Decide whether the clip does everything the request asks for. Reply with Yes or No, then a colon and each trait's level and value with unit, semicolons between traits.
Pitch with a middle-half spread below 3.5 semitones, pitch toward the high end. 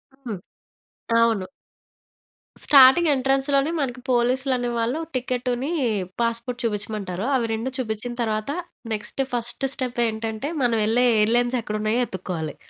Yes: average, 2.9 semitones; high, 240 Hz